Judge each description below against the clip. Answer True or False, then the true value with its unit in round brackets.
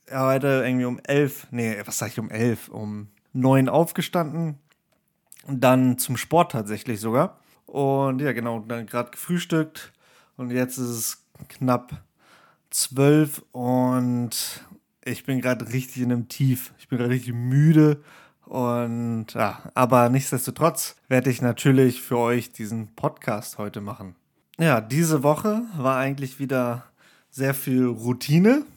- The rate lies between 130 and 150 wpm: True (140 wpm)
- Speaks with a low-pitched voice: True (130 Hz)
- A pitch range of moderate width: True (3.1 semitones)